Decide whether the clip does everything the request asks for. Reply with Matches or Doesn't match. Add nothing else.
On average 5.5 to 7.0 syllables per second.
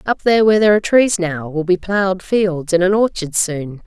Matches